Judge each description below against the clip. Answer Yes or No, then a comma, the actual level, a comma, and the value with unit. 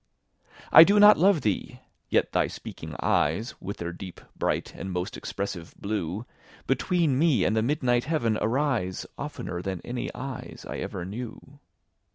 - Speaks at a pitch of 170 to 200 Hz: No, low, 115 Hz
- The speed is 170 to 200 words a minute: No, average, 155 wpm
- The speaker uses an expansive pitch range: Yes, wide, 7.2 semitones